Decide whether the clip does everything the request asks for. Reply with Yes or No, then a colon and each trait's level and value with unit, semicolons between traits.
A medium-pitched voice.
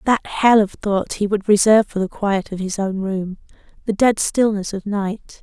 No: high, 205 Hz